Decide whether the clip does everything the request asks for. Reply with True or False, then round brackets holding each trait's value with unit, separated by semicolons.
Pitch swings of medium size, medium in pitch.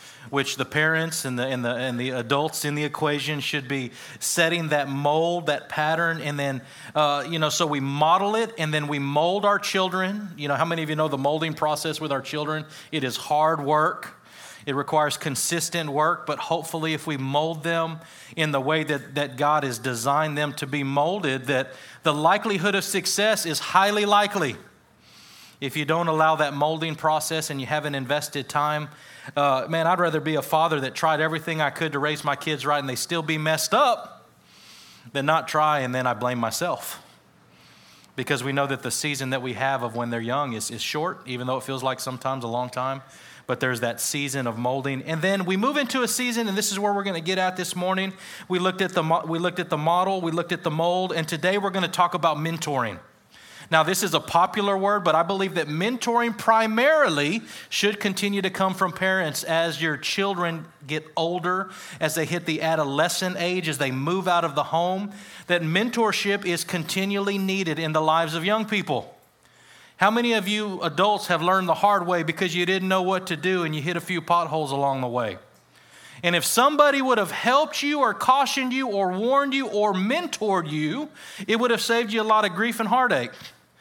True (4.5 semitones; 160 Hz)